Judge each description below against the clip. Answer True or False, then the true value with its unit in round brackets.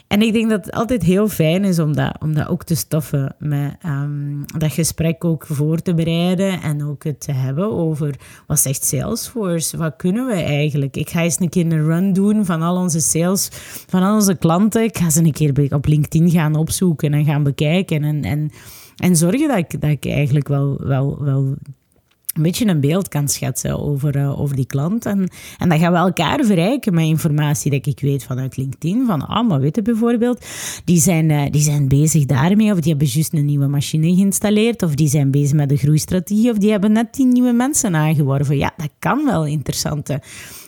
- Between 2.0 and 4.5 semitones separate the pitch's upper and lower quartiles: True (4.1 semitones)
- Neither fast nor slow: False (210 wpm)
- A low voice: False (155 Hz)